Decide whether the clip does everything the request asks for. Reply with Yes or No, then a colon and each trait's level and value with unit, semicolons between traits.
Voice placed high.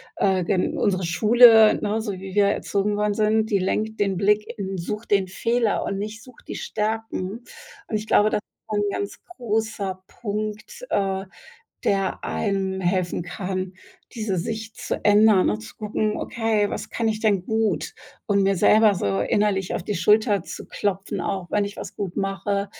Yes: high, 205 Hz